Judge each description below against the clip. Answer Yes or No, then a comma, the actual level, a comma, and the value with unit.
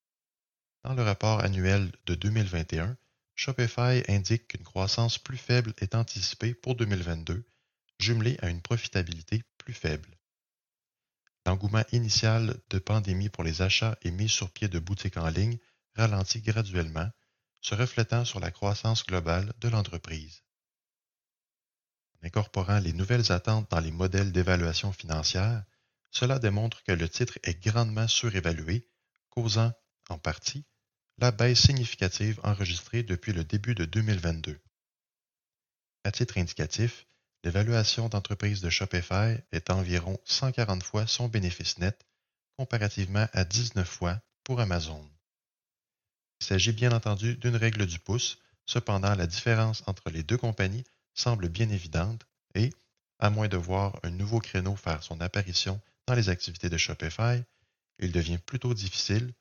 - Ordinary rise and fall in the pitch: Yes, average, 4.2 semitones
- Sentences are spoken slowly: Yes, slow, 135 wpm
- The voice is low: Yes, low, 105 Hz